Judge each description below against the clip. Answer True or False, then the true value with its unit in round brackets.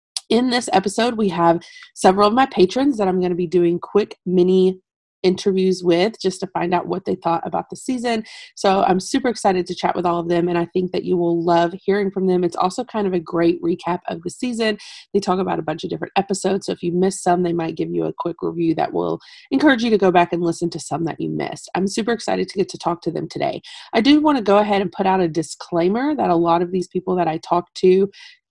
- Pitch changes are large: False (3.0 semitones)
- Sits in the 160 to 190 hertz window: True (185 Hz)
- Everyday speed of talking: False (260 wpm)